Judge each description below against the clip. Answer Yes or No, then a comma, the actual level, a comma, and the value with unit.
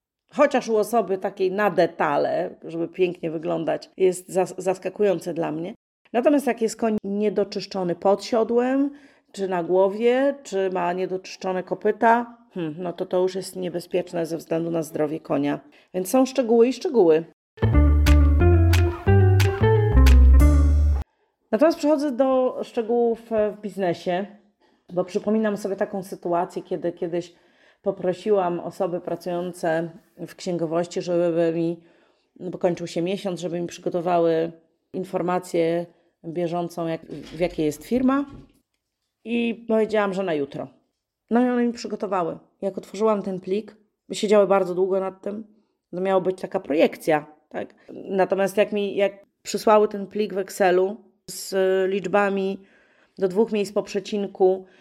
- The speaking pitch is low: No, high, 190 Hz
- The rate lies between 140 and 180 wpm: No, average, 130 wpm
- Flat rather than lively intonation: No, average, 3.4 semitones